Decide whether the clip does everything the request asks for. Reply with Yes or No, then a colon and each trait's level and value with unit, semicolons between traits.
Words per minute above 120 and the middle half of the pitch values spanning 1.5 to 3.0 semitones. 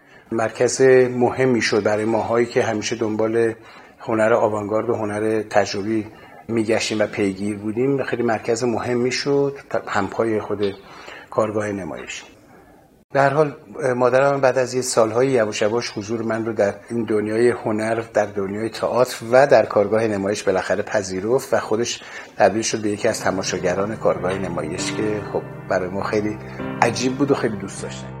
Yes: average, 150 wpm; average, 2.7 semitones